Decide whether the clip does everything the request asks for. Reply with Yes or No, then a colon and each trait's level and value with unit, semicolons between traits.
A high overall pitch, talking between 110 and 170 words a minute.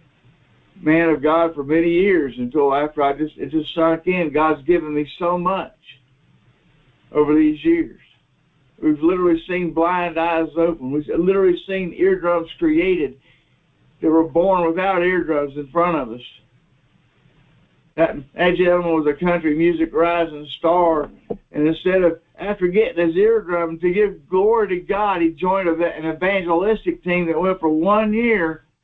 No: medium, 170 Hz; average, 150 wpm